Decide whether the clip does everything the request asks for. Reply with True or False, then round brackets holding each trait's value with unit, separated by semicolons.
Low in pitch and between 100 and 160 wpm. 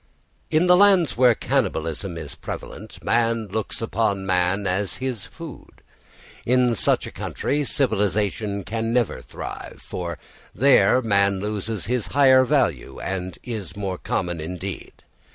True (110 Hz; 135 wpm)